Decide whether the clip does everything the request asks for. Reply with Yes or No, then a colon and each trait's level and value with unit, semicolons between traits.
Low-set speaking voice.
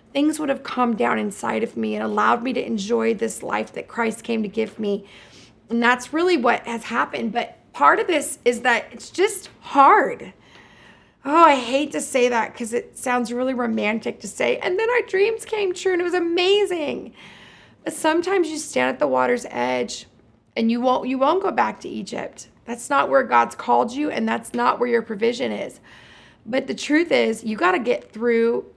No: high, 245 Hz